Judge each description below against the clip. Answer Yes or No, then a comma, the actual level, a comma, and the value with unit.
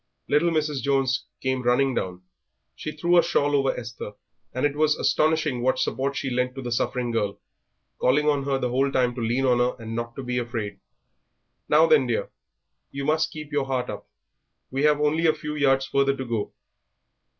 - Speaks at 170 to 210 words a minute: Yes, average, 195 wpm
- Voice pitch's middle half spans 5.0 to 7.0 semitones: No, average, 3.3 semitones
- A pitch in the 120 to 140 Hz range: Yes, low, 135 Hz